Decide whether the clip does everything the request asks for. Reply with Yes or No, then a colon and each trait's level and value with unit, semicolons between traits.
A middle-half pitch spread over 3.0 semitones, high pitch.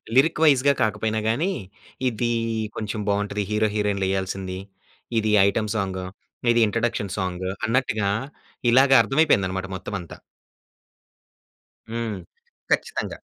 No: average, 3.4 semitones; low, 105 Hz